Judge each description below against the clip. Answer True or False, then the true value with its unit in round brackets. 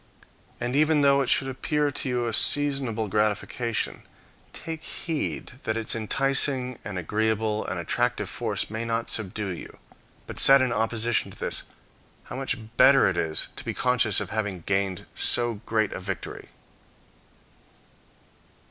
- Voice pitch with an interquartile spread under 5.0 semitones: True (4.0 semitones)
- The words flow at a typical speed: True (150 wpm)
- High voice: False (115 Hz)